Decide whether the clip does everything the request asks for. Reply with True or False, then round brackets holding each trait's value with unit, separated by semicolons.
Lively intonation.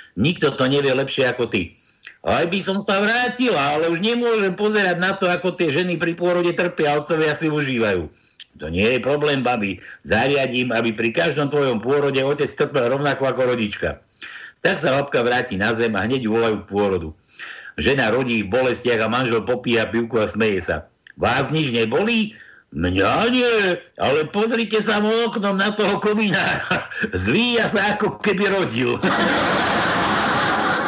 True (8.4 semitones)